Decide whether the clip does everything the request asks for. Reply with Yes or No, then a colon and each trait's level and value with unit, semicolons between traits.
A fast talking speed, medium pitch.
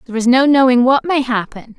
No: fast, 235 wpm; very high, 250 Hz